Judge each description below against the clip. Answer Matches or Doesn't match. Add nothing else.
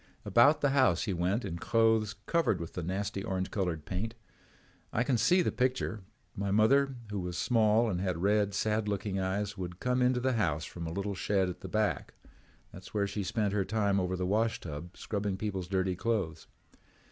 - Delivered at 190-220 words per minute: Matches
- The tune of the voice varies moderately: Matches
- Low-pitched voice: Matches